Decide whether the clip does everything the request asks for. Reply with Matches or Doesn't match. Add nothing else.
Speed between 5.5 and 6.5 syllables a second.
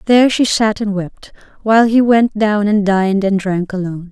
Doesn't match